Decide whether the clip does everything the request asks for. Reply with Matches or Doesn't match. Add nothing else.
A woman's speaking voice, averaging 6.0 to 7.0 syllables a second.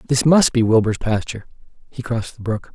Doesn't match